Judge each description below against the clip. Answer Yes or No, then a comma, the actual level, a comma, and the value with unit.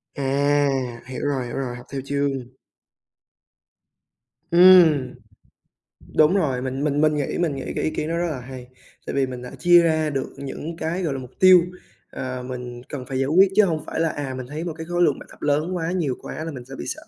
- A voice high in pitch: No, medium, 145 Hz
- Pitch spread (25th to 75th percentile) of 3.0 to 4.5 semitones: Yes, average, 3.8 semitones